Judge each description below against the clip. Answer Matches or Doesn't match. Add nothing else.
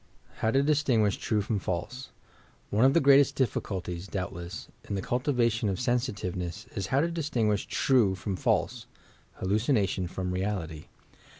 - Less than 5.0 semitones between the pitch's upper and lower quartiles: Doesn't match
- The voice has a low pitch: Matches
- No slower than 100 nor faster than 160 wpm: Matches